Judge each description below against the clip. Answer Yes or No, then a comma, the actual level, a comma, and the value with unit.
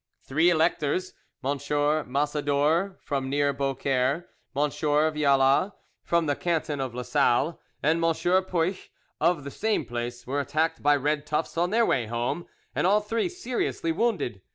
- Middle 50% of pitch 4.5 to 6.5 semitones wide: No, average, 3.7 semitones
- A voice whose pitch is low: No, medium, 150 Hz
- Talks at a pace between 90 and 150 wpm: Yes, average, 140 wpm